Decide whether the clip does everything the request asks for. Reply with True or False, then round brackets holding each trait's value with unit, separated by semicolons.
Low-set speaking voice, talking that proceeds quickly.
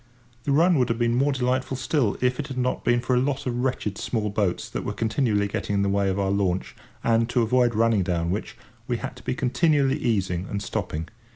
True (115 Hz; 230 wpm)